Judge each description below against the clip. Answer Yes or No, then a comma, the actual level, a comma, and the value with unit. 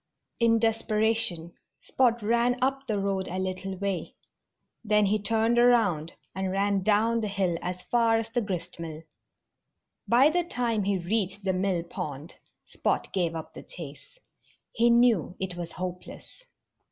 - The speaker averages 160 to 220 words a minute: No, average, 150 wpm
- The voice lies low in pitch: No, high, 200 Hz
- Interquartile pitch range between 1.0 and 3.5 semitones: No, average, 4.0 semitones